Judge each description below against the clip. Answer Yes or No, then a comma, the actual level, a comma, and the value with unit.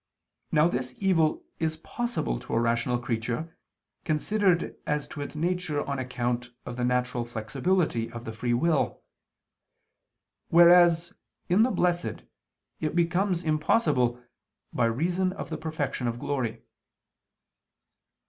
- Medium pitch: Yes, medium, 150 Hz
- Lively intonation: Yes, wide, 6.0 semitones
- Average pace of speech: No, slow, 125 wpm